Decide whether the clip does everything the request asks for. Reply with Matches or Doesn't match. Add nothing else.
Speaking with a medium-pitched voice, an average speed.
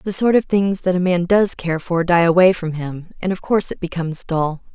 Doesn't match